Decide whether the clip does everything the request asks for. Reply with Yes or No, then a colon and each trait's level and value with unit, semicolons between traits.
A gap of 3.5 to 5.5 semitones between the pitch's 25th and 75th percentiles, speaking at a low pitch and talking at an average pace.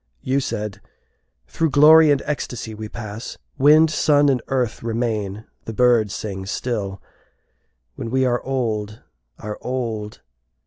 No: average, 4.0 semitones; low, 120 Hz; slow, 130 wpm